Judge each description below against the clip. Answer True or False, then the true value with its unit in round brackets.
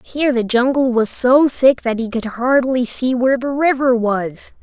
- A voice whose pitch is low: False (250 Hz)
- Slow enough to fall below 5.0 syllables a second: True (4.5 syllables/s)